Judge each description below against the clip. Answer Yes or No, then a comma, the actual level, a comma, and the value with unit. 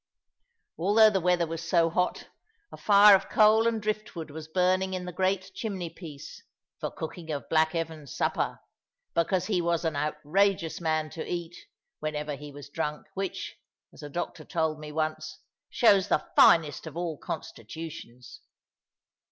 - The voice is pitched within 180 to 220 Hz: No, medium, 165 Hz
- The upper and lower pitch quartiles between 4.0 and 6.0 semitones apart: No, average, 3.4 semitones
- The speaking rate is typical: Yes, average, 155 wpm